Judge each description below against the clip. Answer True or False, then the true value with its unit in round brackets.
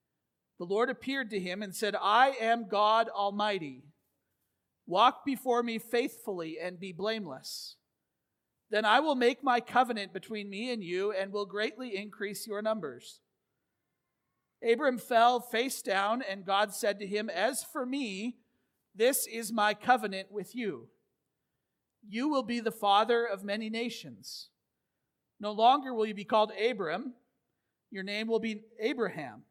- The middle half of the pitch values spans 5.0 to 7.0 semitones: False (2.9 semitones)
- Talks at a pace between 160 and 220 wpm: False (145 wpm)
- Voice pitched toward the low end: False (220 Hz)